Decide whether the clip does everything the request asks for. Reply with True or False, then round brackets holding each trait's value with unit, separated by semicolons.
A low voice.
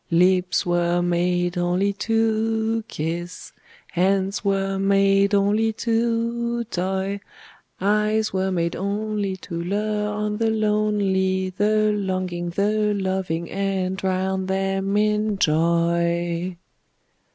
False (195 Hz)